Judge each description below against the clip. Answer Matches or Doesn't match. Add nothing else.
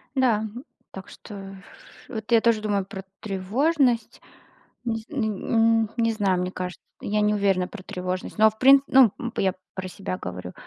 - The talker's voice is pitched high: Matches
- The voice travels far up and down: Doesn't match